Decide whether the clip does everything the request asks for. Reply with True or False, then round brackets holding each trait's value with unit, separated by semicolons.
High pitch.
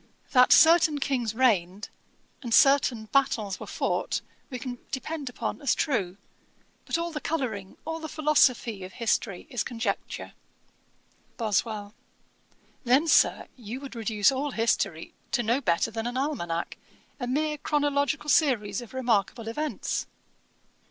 True (245 Hz)